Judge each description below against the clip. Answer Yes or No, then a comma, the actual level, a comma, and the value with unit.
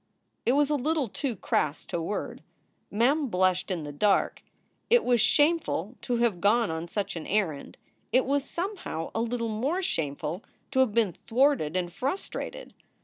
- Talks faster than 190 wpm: No, average, 165 wpm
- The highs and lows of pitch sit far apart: Yes, wide, 7.3 semitones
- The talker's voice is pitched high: Yes, high, 230 Hz